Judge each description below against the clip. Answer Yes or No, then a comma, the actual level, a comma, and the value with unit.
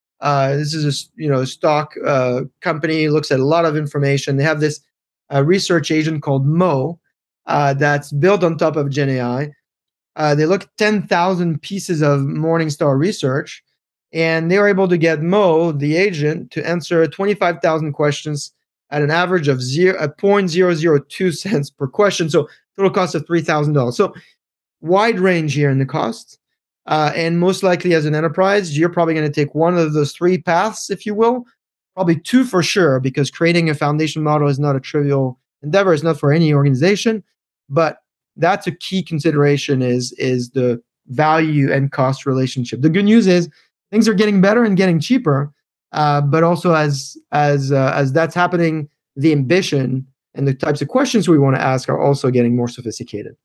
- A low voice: No, medium, 155 Hz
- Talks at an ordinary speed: Yes, average, 180 wpm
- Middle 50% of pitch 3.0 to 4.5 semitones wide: Yes, average, 3.9 semitones